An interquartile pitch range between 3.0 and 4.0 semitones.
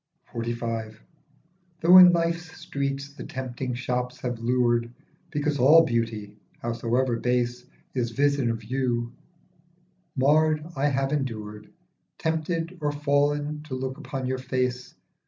Yes: average, 3.7 semitones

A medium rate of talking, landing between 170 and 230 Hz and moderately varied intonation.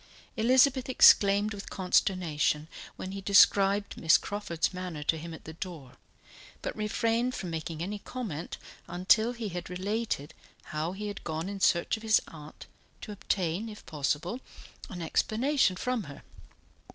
Yes: average, 150 wpm; high, 190 Hz; average, 4.7 semitones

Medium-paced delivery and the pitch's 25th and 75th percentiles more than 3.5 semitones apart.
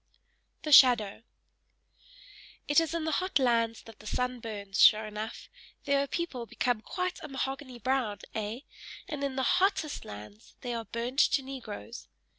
Yes: average, 160 wpm; average, 4.2 semitones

